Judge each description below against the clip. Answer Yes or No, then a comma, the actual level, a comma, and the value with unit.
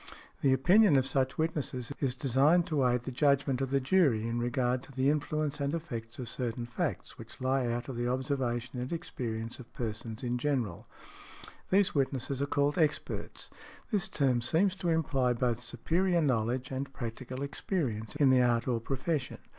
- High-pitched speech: No, low, 130 Hz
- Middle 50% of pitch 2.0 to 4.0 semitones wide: Yes, average, 3.1 semitones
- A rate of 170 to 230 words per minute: Yes, average, 175 wpm